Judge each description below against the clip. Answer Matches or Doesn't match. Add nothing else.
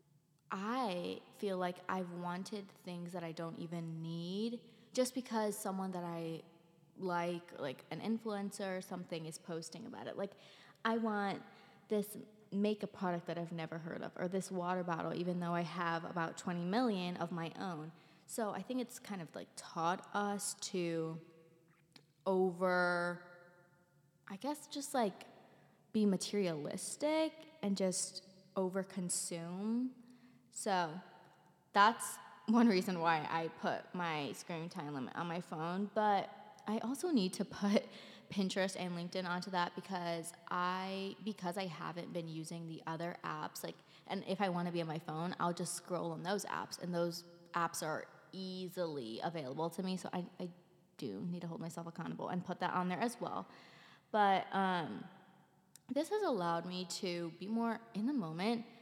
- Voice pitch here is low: Doesn't match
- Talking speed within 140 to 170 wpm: Matches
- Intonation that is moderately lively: Matches